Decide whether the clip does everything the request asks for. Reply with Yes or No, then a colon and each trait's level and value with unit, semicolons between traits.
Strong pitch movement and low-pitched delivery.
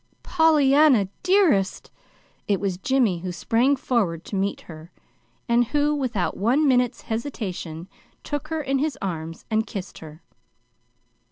No: wide, 7.4 semitones; high, 235 Hz